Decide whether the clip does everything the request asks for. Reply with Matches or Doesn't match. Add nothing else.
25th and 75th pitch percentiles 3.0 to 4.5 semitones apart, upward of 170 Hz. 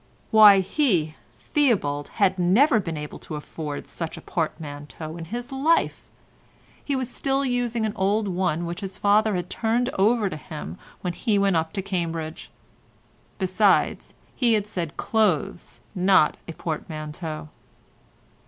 Doesn't match